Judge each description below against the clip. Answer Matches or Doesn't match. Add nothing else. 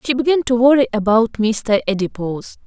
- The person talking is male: Doesn't match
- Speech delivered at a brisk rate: Doesn't match